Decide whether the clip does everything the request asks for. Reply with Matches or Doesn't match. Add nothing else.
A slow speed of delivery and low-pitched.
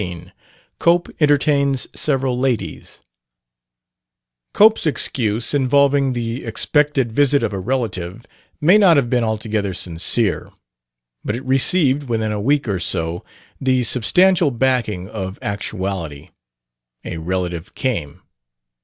Matches